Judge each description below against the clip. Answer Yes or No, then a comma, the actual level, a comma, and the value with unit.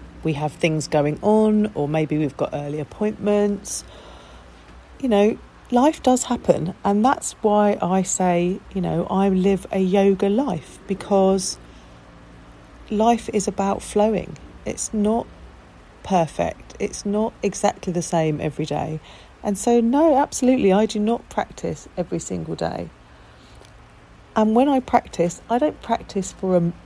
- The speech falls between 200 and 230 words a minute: No, average, 140 wpm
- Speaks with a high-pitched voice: Yes, high, 195 Hz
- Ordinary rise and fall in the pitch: Yes, average, 4.9 semitones